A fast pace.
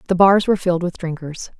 Yes: fast, 225 wpm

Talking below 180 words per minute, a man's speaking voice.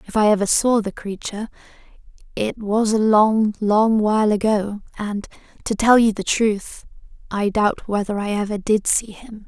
No: average, 170 wpm; female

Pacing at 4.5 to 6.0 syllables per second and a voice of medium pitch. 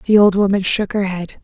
No: 5.5 syllables/s; high, 195 Hz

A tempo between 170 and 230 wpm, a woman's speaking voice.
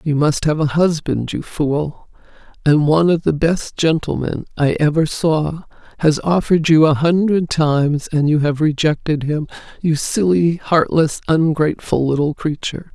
No: average, 155 wpm; female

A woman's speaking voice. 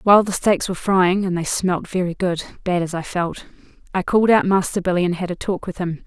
Yes: female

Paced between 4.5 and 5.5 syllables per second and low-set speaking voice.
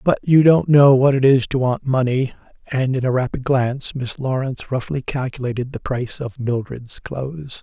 Yes: 5.0 syllables/s; low, 130 Hz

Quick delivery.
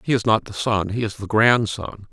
Yes: fast, 255 wpm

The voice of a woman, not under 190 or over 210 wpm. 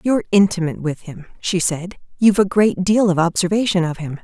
Yes: female; average, 200 wpm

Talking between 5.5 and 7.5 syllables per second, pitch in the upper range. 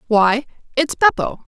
No: 4.0 syllables/s; very high, 260 Hz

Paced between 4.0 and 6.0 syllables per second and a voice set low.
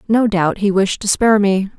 No: 5.1 syllables/s; high, 200 Hz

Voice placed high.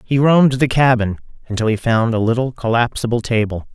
No: low, 120 Hz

